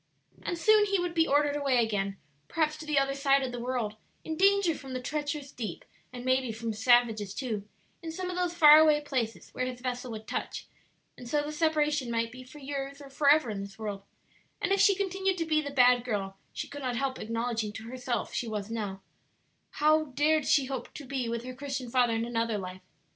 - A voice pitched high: Yes, very high, 260 Hz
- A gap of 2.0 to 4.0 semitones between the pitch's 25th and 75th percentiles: No, average, 4.7 semitones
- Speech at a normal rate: No, fast, 220 wpm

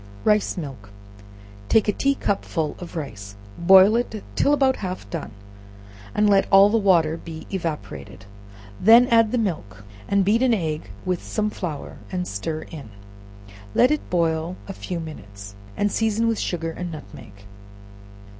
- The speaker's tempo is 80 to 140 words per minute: No, average, 155 wpm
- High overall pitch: No, medium, 180 Hz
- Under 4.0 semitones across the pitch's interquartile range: No, average, 5.1 semitones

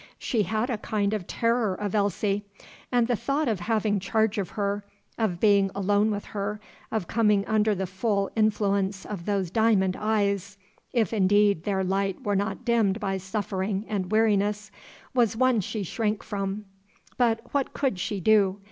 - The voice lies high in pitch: Yes, high, 205 Hz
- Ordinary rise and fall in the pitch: No, narrow, 2.0 semitones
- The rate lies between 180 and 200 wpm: No, average, 165 wpm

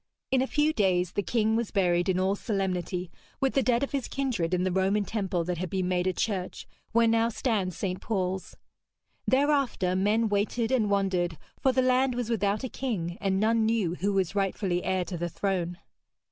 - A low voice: No, high, 200 Hz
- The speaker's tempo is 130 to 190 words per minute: No, average, 200 wpm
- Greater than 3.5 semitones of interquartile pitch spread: Yes, average, 4.0 semitones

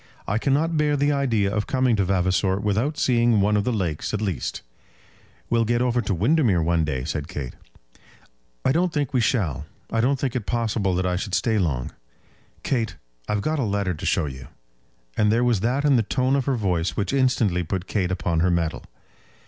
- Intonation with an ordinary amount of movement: No, wide, 5.7 semitones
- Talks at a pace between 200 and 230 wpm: Yes, fast, 205 wpm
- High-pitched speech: No, low, 105 Hz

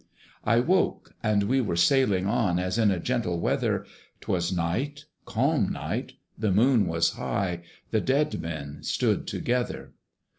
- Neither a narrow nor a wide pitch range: No, wide, 6.1 semitones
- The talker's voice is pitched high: No, low, 105 Hz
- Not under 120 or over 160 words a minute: Yes, average, 145 wpm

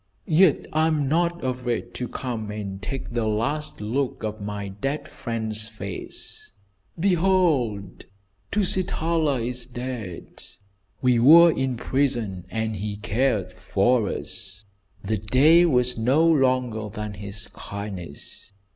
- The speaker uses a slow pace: Yes, slow, 120 wpm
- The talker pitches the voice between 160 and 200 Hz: No, low, 120 Hz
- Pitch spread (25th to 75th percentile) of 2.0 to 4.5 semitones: No, average, 5.2 semitones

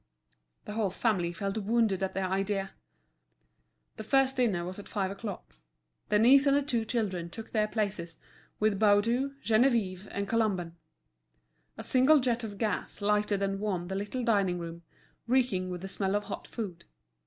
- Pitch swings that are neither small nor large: Yes, average, 3.2 semitones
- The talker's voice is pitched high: Yes, high, 205 Hz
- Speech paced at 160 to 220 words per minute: Yes, average, 165 wpm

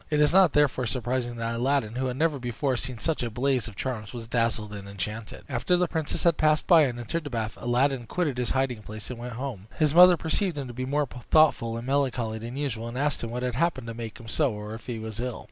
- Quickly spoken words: Yes, fast, 250 wpm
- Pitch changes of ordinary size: Yes, average, 3.9 semitones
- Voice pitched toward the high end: No, low, 125 Hz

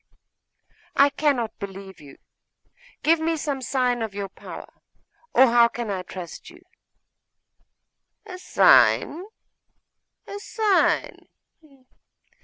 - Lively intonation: Yes, wide, 8.0 semitones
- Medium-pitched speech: No, very high, 250 Hz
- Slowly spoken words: Yes, slow, 100 wpm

